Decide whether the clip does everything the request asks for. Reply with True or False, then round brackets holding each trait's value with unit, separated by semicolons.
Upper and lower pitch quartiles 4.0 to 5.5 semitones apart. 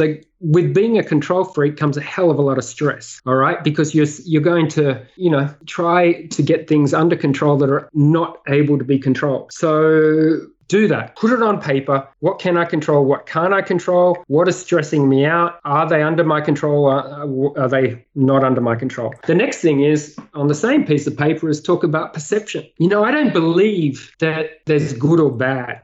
False (3.2 semitones)